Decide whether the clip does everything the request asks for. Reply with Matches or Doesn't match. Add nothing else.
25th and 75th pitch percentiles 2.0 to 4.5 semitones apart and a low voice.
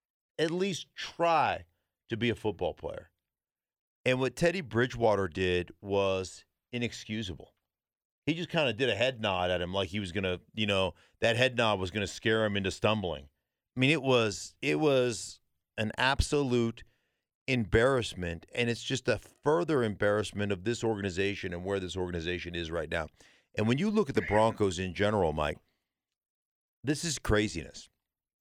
Doesn't match